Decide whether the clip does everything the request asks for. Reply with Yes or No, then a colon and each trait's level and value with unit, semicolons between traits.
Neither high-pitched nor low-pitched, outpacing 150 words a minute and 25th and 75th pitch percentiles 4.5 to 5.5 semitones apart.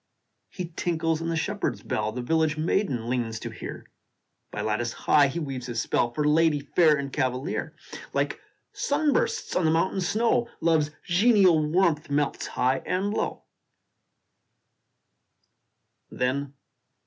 No: medium, 155 Hz; average, 140 wpm; average, 5.0 semitones